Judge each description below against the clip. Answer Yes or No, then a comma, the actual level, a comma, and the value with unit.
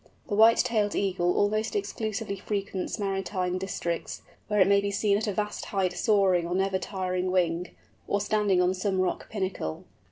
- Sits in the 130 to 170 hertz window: No, high, 195 Hz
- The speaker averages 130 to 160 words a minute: No, average, 170 wpm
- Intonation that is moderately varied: No, narrow, 2.1 semitones